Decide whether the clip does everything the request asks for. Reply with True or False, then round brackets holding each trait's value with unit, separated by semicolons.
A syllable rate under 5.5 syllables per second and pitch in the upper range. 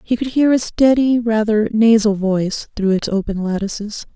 True (4.9 syllables/s; 220 Hz)